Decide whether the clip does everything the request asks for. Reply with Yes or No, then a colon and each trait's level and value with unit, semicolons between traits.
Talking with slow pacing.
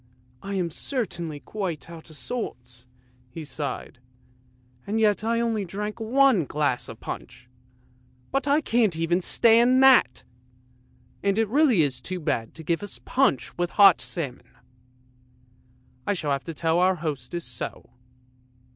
No: average, 150 wpm